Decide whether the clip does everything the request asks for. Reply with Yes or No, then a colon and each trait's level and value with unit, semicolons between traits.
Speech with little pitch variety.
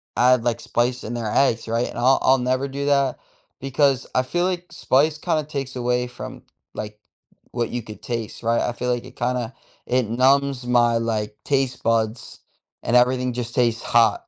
Yes: narrow, 2.3 semitones